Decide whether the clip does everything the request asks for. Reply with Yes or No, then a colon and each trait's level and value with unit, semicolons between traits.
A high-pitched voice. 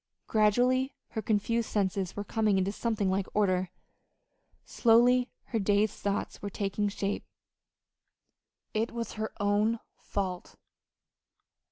Yes: high, 210 Hz